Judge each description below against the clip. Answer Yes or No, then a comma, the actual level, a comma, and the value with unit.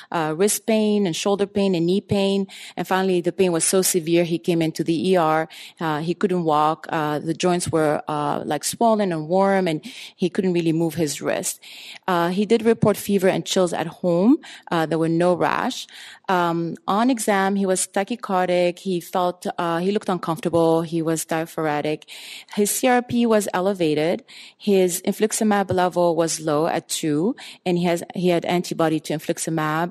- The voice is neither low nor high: Yes, medium, 180 Hz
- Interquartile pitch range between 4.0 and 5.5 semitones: No, average, 3.2 semitones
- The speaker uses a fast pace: No, average, 180 wpm